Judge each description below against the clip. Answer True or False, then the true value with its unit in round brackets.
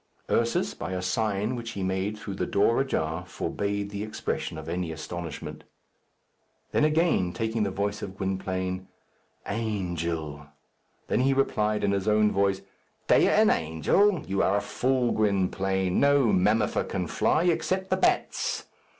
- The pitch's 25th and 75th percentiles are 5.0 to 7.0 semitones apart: False (3.4 semitones)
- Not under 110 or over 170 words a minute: True (150 wpm)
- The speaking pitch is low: True (100 Hz)